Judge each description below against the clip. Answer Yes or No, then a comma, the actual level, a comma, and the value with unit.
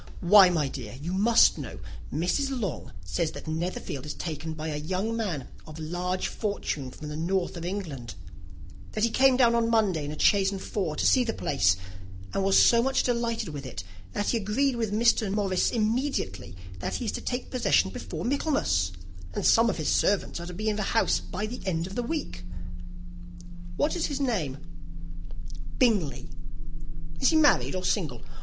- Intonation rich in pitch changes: Yes, wide, 6.8 semitones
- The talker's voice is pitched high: Yes, high, 195 Hz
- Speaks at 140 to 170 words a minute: No, average, 190 wpm